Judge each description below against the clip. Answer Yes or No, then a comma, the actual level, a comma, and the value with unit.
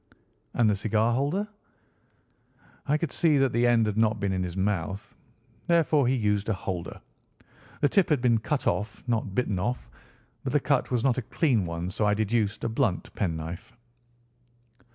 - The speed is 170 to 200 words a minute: Yes, average, 180 wpm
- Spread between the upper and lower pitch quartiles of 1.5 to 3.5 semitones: No, average, 4.6 semitones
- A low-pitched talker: Yes, low, 110 Hz